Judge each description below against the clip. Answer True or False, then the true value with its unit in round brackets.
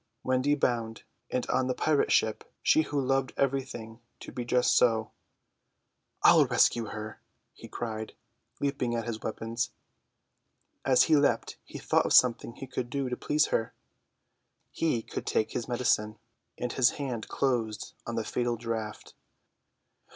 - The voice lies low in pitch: True (120 Hz)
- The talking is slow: False (145 wpm)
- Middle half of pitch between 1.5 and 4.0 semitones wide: True (2.8 semitones)